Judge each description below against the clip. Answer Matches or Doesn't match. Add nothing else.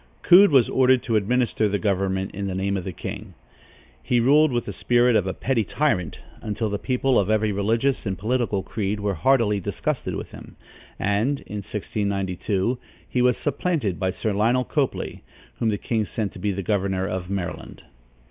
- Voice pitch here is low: Matches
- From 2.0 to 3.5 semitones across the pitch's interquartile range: Doesn't match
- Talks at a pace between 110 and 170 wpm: Doesn't match